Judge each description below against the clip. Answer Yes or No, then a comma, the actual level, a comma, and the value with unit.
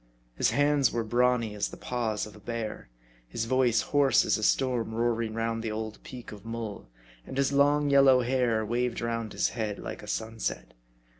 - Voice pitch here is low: Yes, low, 115 Hz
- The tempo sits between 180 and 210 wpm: Yes, average, 190 wpm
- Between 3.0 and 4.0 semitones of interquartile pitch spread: No, narrow, 2.5 semitones